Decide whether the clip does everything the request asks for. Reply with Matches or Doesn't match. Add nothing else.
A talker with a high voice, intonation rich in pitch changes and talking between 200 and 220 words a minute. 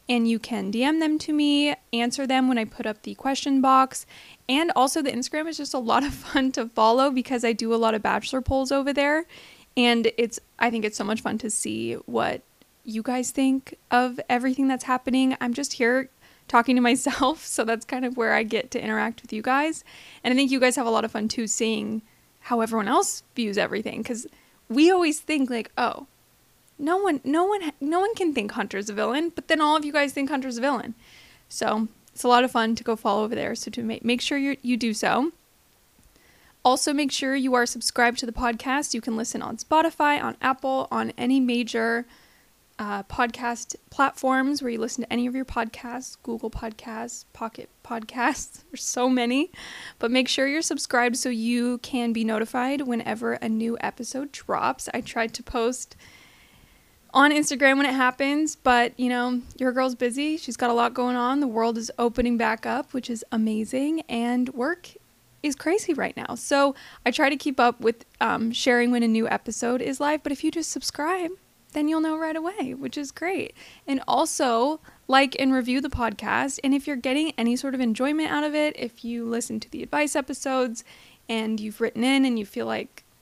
Doesn't match